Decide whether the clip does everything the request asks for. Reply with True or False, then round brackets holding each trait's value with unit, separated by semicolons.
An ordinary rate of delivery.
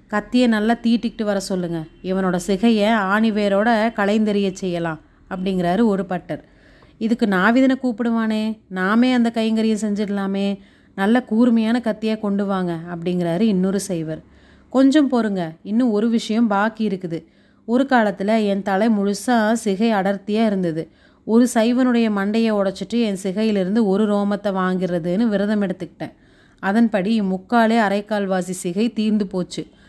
True (120 wpm)